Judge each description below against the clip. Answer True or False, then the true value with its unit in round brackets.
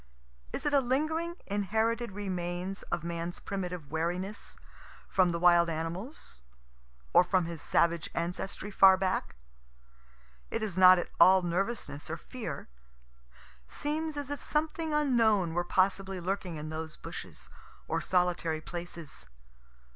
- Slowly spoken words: True (130 wpm)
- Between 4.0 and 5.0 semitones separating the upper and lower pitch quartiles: True (4.5 semitones)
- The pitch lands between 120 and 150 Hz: False (185 Hz)